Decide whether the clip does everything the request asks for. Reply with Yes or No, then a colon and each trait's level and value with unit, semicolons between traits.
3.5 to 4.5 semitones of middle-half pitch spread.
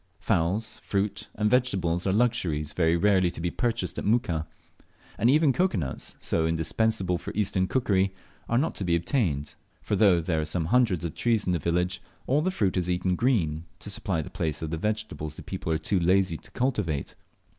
No: average, 4.9 semitones